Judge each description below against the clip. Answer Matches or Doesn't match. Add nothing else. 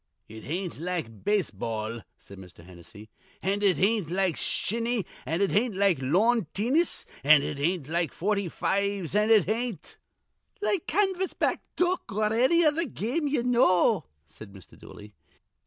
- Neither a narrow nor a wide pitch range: Doesn't match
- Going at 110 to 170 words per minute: Matches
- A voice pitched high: Matches